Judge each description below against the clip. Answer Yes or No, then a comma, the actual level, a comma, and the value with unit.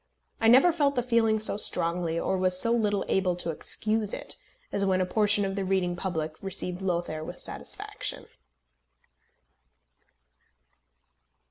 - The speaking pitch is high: Yes, high, 195 Hz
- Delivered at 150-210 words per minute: No, average, 140 wpm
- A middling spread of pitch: Yes, average, 3.5 semitones